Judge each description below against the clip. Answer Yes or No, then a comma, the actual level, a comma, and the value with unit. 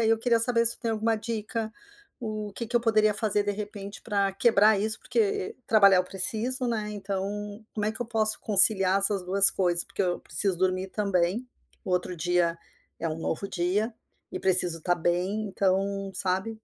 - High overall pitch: Yes, high, 205 Hz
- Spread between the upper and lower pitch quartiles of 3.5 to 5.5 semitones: No, average, 2.9 semitones